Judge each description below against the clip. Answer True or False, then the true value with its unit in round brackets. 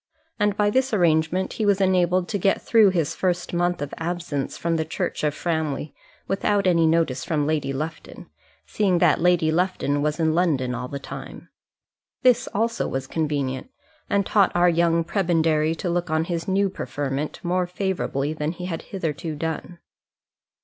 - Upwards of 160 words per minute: True (170 wpm)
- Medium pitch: True (170 Hz)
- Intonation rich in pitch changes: False (3.2 semitones)